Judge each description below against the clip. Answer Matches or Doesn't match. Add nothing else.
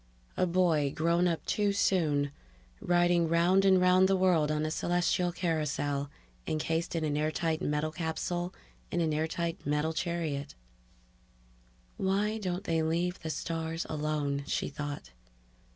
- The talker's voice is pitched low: Doesn't match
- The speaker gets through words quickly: Doesn't match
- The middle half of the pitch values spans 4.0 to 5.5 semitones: Doesn't match